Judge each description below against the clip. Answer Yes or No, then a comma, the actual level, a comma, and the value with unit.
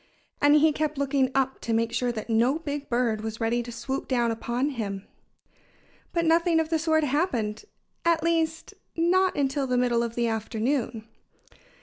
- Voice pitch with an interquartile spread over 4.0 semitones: Yes, average, 5.1 semitones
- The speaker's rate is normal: Yes, average, 170 wpm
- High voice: Yes, very high, 265 Hz